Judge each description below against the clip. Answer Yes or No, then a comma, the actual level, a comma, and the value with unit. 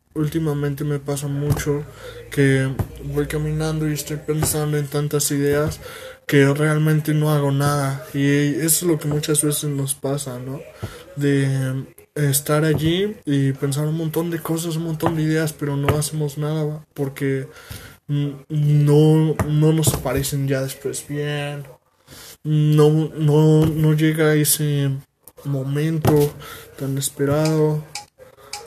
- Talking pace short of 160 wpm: Yes, average, 130 wpm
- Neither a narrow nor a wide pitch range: No, narrow, 1.5 semitones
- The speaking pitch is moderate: Yes, medium, 150 Hz